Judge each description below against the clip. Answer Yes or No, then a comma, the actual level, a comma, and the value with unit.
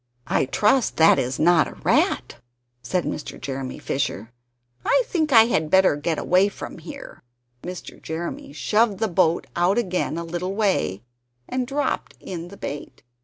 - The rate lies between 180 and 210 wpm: No, average, 160 wpm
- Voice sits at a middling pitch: Yes, medium, 175 Hz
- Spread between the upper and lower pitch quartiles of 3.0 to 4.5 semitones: No, average, 4.9 semitones